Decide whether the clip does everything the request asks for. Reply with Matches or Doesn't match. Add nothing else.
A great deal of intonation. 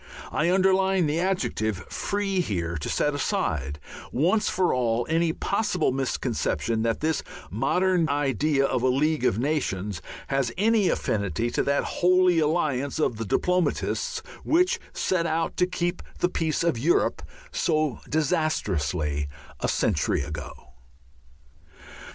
Matches